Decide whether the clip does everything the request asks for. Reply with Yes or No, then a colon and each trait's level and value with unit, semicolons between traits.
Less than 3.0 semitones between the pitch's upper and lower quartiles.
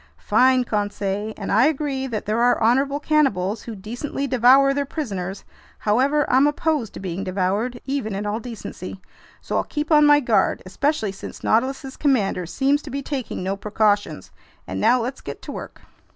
No: average, 5.2 semitones